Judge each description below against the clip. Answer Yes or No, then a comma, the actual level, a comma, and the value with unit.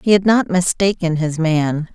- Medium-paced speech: Yes, average, 185 wpm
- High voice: No, medium, 175 Hz